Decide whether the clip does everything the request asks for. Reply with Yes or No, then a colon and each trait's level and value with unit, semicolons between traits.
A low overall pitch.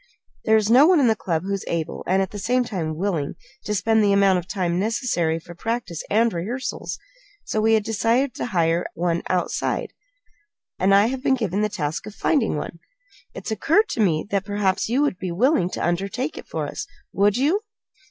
No: high, 205 Hz